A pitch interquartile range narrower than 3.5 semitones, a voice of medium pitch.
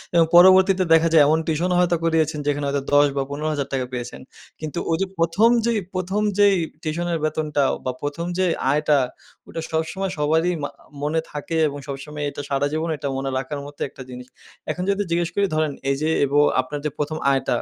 Yes: average, 3.0 semitones; medium, 155 Hz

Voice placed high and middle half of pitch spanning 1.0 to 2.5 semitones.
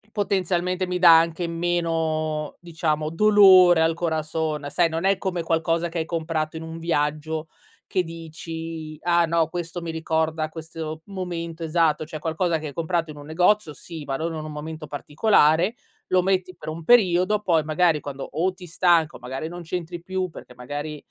No: medium, 165 Hz; narrow, 2.0 semitones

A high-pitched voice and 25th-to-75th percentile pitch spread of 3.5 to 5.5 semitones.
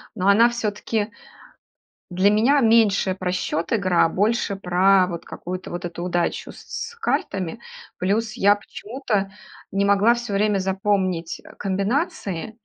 No: high, 200 Hz; average, 2.9 semitones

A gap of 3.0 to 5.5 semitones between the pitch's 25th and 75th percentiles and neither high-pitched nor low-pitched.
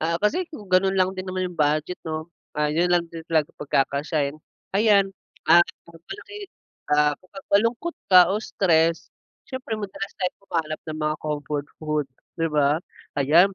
Yes: average, 4.2 semitones; medium, 170 Hz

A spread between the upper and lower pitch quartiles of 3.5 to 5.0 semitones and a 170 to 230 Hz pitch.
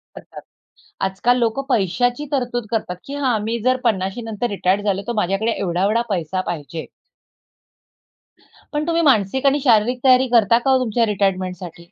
Yes: average, 4.5 semitones; high, 220 Hz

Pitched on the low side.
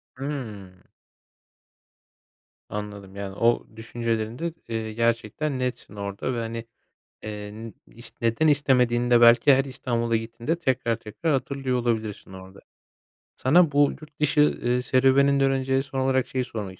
Yes: low, 120 Hz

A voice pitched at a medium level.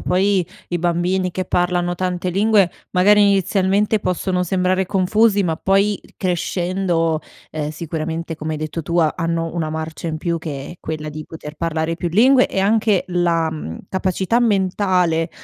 Yes: medium, 175 Hz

